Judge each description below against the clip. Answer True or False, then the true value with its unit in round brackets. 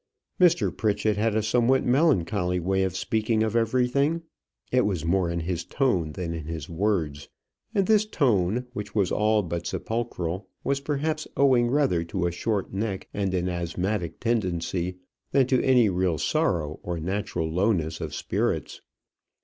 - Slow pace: False (155 wpm)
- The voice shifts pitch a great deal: True (5.8 semitones)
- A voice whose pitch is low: True (100 Hz)